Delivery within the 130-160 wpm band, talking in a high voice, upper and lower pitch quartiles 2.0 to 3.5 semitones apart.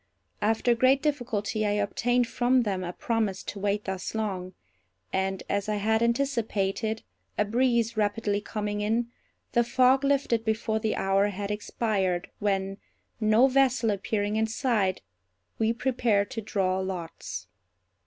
Yes: average, 140 wpm; high, 215 Hz; average, 2.9 semitones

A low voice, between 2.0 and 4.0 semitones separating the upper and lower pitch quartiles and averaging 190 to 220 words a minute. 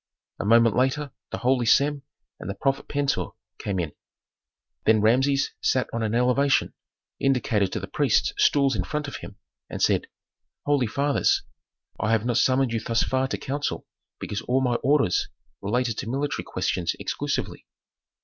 No: low, 125 Hz; average, 3.6 semitones; average, 160 wpm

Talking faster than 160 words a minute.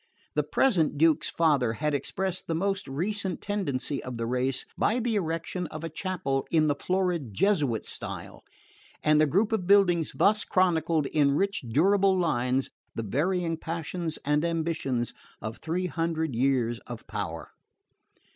No: average, 150 wpm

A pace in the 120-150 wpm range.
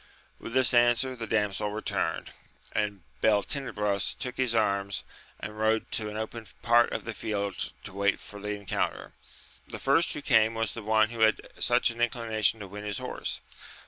No: average, 175 wpm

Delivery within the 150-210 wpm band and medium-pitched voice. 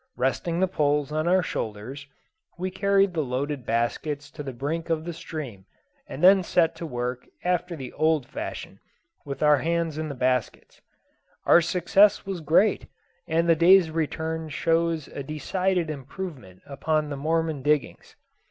Yes: average, 155 wpm; medium, 155 Hz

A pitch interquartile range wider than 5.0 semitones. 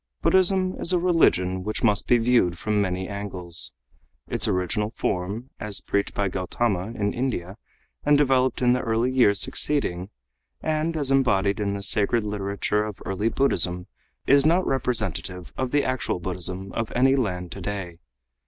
Yes: wide, 5.6 semitones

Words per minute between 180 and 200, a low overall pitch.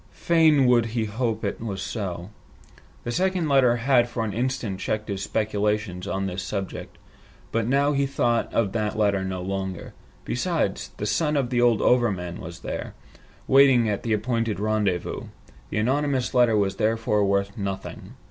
No: average, 165 wpm; low, 110 Hz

